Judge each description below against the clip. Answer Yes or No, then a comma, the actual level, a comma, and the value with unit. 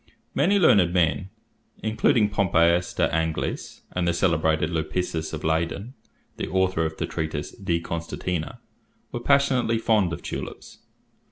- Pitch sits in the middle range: No, very low, 85 Hz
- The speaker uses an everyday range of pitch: Yes, average, 4.2 semitones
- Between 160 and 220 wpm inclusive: No, slow, 135 wpm